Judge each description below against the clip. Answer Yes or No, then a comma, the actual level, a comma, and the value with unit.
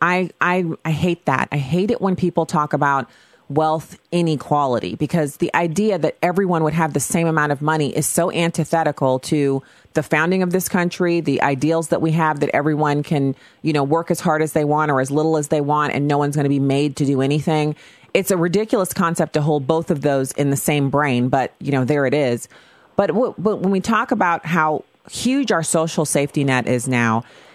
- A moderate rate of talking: No, fast, 225 wpm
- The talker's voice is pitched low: No, medium, 155 Hz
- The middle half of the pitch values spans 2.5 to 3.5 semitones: Yes, average, 3.0 semitones